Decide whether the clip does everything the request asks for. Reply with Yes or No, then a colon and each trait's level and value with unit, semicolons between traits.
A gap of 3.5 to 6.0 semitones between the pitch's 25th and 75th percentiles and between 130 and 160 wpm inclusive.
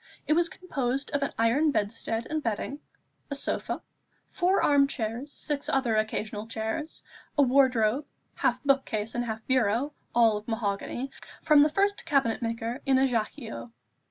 Yes: average, 4.3 semitones; average, 155 wpm